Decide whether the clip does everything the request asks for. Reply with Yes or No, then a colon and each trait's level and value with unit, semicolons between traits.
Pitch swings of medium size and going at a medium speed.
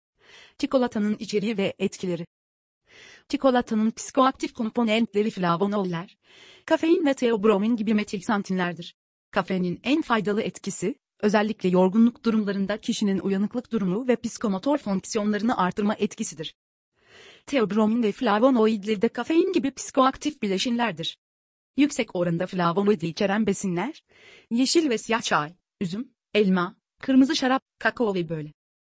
Yes: average, 4.1 semitones; average, 110 wpm